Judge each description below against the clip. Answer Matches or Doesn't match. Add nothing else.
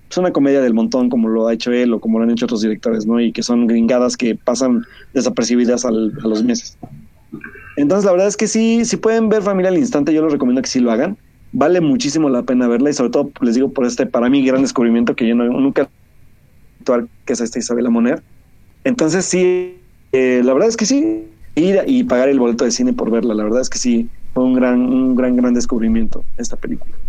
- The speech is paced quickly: Matches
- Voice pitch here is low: Matches